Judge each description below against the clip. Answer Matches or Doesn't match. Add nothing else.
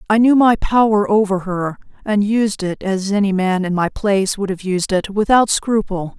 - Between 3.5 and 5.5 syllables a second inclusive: Doesn't match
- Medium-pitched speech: Doesn't match